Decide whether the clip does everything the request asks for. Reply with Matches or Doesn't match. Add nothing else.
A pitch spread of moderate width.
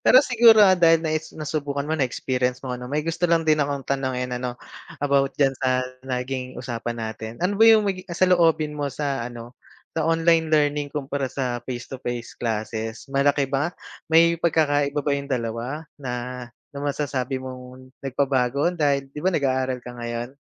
Matches